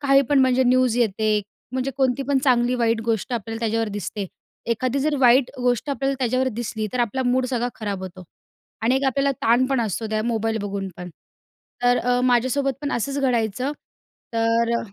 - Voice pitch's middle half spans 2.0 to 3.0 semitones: Yes, narrow, 2.6 semitones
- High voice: Yes, high, 245 Hz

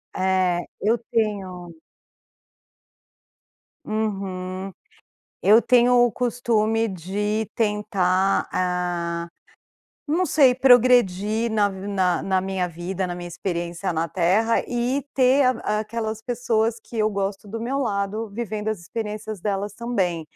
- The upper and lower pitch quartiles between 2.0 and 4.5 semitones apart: Yes, average, 3.6 semitones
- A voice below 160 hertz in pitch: No, high, 210 Hz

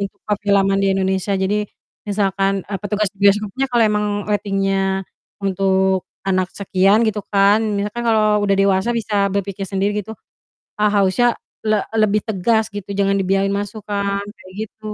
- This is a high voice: Yes, high, 200 Hz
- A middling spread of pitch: No, narrow, 1.3 semitones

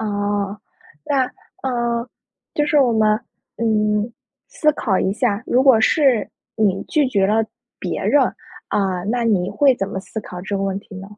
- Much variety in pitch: No, average, 3.6 semitones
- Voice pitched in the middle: No, high, 215 Hz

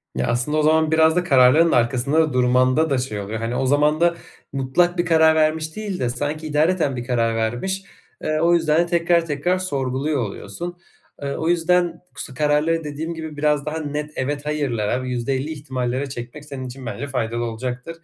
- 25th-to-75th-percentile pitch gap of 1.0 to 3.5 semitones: No, average, 4.0 semitones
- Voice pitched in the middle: Yes, medium, 145 Hz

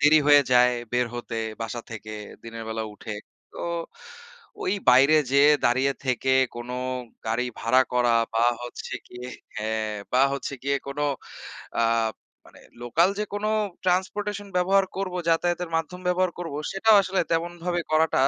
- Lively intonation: Yes, wide, 6.6 semitones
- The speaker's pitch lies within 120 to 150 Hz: Yes, medium, 140 Hz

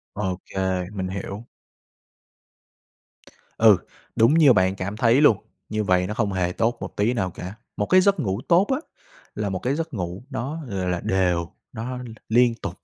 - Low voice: Yes, low, 105 Hz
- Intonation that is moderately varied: Yes, average, 5.0 semitones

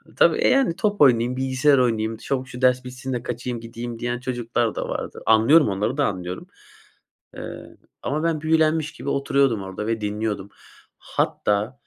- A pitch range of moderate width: Yes, average, 3.7 semitones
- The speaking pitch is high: No, low, 125 Hz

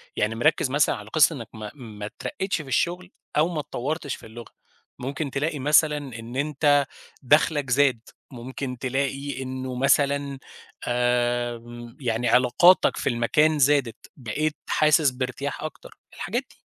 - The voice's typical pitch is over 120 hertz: Yes, low, 135 Hz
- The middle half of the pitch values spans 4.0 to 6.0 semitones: No, average, 3.4 semitones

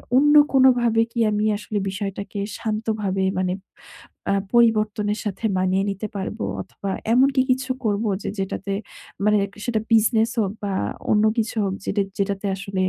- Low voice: No, high, 210 Hz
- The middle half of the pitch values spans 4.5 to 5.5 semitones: No, narrow, 2.4 semitones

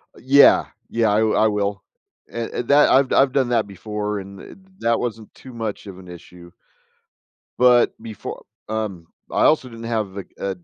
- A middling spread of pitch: Yes, average, 3.0 semitones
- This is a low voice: Yes, low, 110 Hz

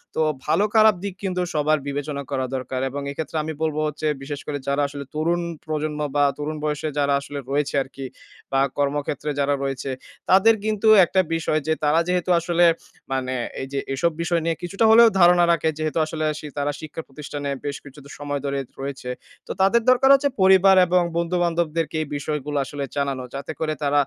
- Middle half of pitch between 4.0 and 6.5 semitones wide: No, average, 3.4 semitones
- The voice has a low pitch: No, medium, 150 Hz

